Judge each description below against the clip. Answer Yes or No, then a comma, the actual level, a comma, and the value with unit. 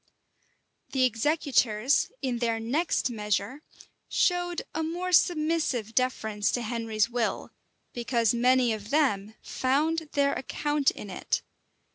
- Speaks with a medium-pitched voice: No, very high, 255 Hz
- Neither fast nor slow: No, slow, 120 wpm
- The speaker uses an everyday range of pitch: Yes, average, 5.0 semitones